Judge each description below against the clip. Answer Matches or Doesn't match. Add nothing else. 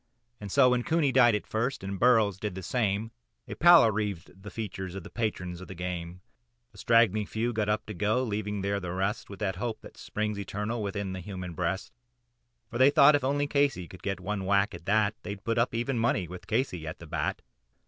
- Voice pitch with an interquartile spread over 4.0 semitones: Doesn't match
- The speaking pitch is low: Matches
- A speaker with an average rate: Doesn't match